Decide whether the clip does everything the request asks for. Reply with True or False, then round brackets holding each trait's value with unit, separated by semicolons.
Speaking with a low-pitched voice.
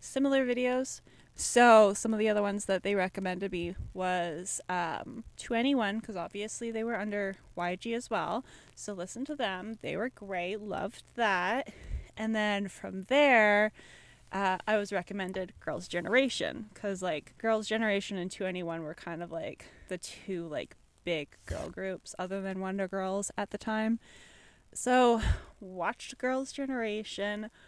False (205 Hz)